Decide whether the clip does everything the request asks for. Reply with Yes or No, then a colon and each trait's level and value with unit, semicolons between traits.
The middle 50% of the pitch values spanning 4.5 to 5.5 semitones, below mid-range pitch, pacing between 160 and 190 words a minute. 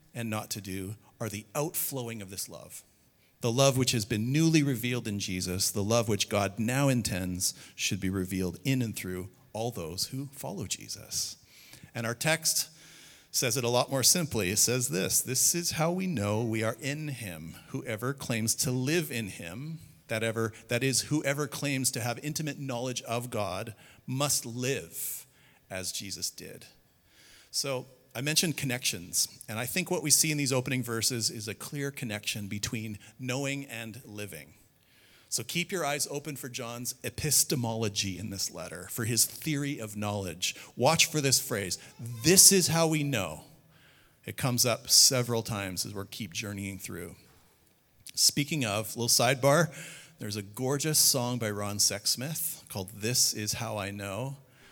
Yes: average, 4.9 semitones; low, 120 Hz; average, 170 wpm